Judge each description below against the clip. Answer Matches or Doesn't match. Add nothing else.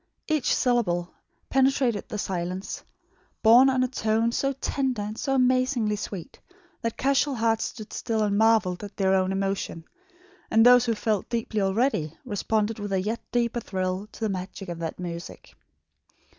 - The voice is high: Matches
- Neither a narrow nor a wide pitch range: Matches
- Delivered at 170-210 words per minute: Doesn't match